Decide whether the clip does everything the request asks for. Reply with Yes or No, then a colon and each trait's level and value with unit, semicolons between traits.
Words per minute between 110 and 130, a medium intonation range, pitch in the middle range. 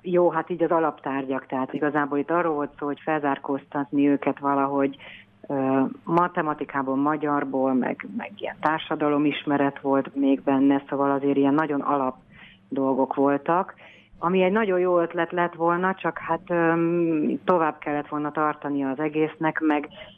No: average, 140 wpm; average, 3.0 semitones; medium, 150 Hz